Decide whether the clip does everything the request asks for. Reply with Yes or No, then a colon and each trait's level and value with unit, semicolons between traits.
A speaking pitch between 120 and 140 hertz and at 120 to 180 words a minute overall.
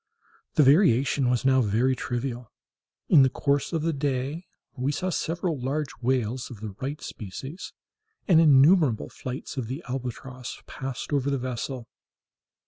Yes: low, 135 Hz; average, 145 wpm